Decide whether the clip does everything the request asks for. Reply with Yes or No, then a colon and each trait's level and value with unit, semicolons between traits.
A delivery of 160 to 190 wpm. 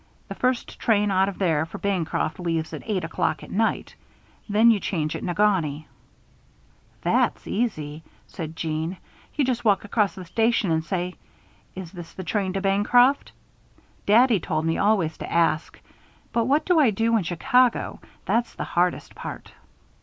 Yes: average, 165 wpm